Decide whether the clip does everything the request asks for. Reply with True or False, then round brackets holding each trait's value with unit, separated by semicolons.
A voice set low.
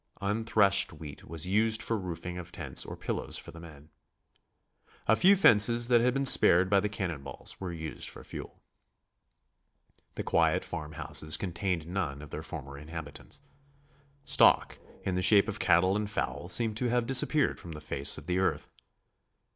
True (90 Hz)